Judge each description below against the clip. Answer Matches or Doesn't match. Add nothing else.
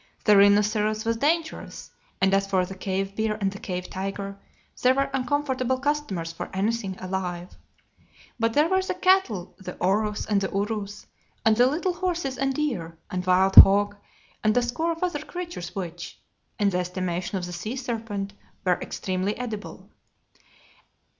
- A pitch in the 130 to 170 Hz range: Doesn't match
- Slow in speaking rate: Doesn't match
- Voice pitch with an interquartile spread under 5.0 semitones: Doesn't match